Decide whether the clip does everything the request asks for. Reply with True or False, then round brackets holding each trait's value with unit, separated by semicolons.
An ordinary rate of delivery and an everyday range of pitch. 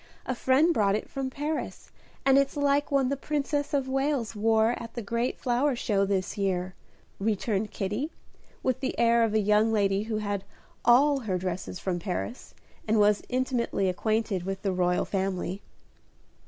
True (170 wpm; 5.0 semitones)